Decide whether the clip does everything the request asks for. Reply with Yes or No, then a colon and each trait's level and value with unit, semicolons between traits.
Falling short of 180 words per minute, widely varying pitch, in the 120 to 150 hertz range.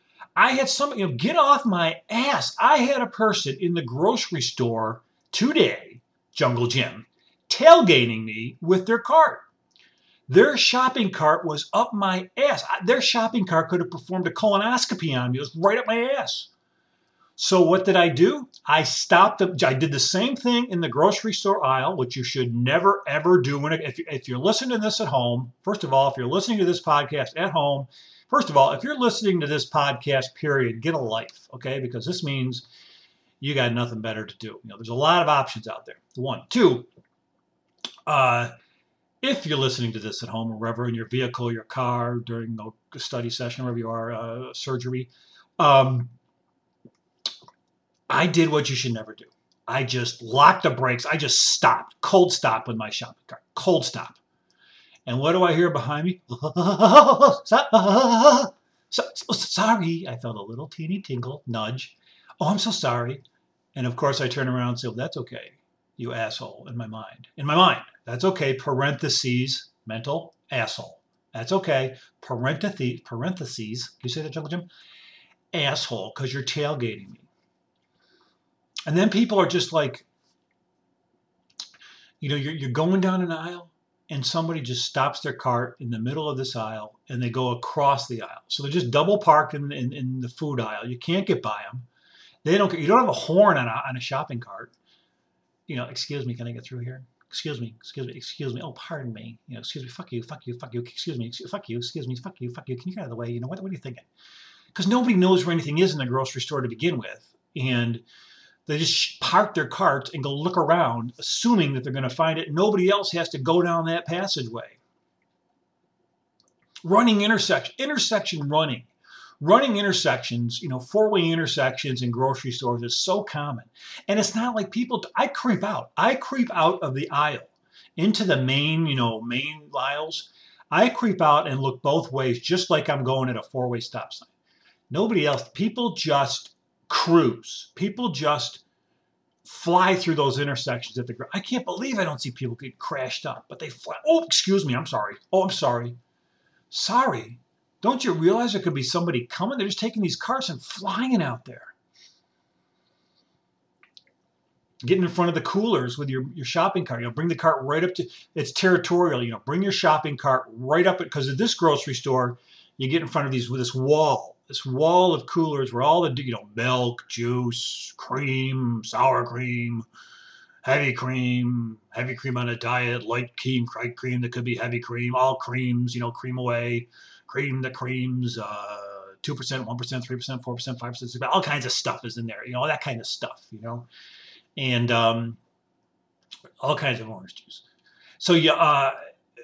No: average, 195 wpm; wide, 6.5 semitones; medium, 140 Hz